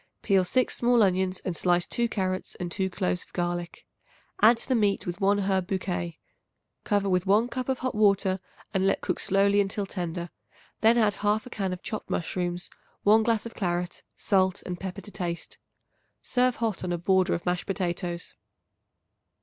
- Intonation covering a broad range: No, average, 2.8 semitones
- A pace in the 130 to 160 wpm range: No, average, 180 wpm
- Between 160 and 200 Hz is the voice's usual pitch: Yes, high, 190 Hz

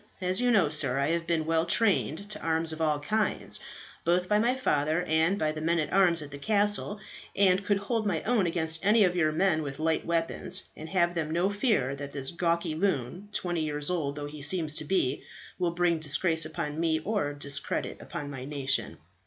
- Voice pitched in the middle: Yes, medium, 165 Hz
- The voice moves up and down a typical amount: Yes, average, 3.8 semitones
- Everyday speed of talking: No, fast, 210 wpm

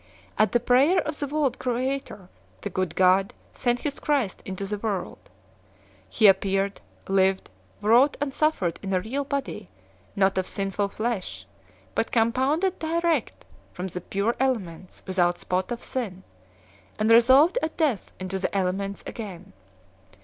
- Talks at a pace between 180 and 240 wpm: No, average, 145 wpm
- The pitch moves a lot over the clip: Yes, wide, 5.9 semitones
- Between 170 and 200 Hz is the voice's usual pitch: No, high, 215 Hz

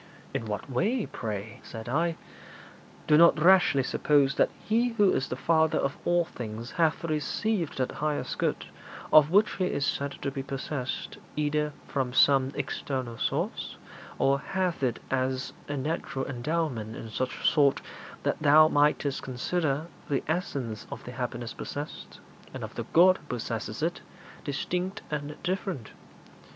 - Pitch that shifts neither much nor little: Yes, average, 4.4 semitones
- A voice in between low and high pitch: Yes, medium, 145 Hz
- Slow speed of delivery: No, average, 150 wpm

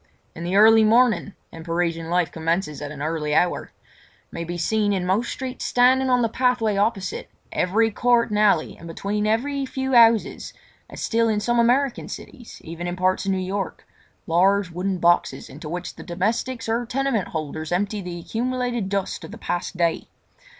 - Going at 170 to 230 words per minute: Yes, average, 175 wpm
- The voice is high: Yes, high, 200 Hz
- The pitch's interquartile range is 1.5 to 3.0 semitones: No, average, 5.1 semitones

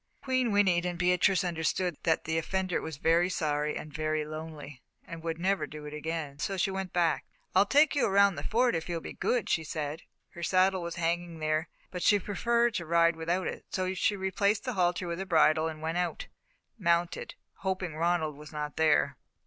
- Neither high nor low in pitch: Yes, medium, 170 Hz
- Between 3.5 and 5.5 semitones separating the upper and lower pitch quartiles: No, average, 3.0 semitones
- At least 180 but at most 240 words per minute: Yes, average, 200 wpm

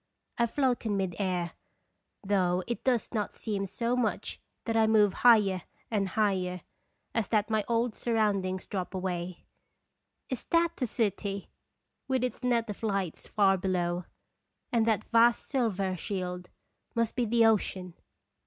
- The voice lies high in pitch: Yes, high, 210 Hz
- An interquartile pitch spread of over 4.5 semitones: No, average, 3.7 semitones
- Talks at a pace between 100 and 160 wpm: Yes, average, 145 wpm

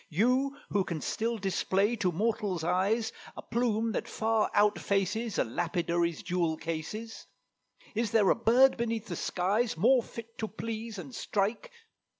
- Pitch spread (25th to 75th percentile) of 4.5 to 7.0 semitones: No, average, 4.0 semitones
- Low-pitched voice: No, high, 215 Hz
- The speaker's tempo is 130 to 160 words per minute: Yes, average, 150 wpm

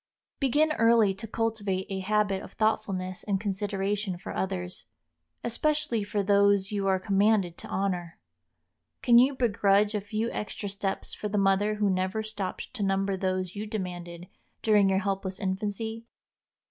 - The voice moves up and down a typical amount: No, narrow, 2.1 semitones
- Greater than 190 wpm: No, average, 150 wpm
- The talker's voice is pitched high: Yes, high, 200 Hz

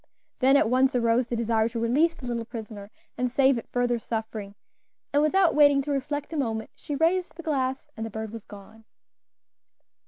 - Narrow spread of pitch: No, average, 4.2 semitones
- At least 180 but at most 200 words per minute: Yes, average, 190 wpm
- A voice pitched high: Yes, high, 245 Hz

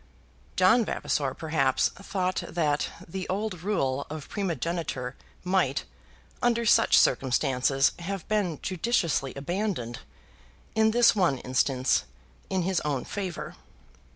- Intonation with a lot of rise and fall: Yes, wide, 6.3 semitones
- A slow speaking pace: Yes, slow, 110 wpm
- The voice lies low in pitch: No, medium, 170 Hz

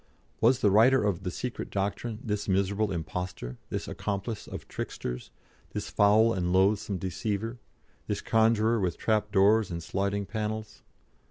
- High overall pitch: No, low, 105 Hz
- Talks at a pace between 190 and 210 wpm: No, average, 145 wpm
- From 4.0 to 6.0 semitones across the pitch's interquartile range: No, narrow, 2.5 semitones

